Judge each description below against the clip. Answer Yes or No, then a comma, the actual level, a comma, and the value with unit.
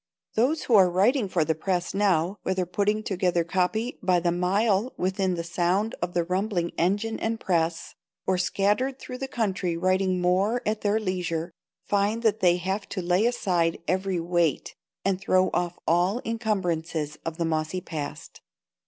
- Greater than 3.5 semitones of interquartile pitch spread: No, average, 3.1 semitones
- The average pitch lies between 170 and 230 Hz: Yes, medium, 185 Hz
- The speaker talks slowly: No, average, 170 wpm